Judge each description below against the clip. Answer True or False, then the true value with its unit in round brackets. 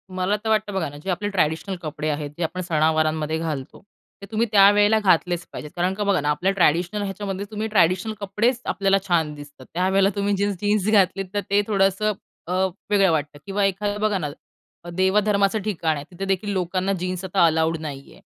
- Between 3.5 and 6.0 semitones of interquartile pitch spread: True (4.0 semitones)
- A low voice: False (190 Hz)